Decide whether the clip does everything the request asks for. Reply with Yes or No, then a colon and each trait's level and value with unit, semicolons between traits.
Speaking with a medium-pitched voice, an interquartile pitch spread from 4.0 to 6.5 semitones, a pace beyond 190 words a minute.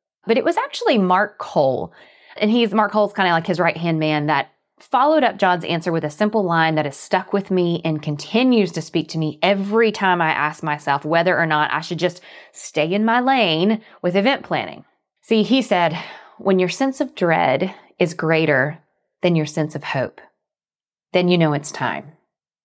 Yes: medium, 180 Hz; average, 4.9 semitones; average, 200 wpm